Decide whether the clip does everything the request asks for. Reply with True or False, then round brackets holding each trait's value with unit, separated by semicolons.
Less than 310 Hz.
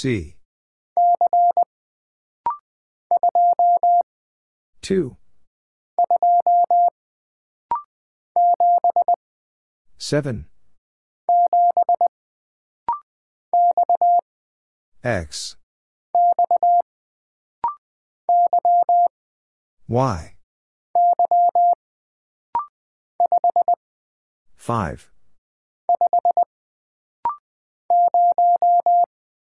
False (350 Hz)